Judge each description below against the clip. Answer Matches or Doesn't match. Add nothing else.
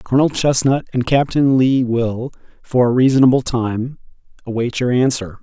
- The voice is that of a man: Matches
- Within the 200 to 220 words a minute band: Doesn't match